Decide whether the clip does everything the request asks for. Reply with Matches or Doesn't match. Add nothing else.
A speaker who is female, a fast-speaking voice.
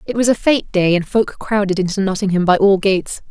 Matches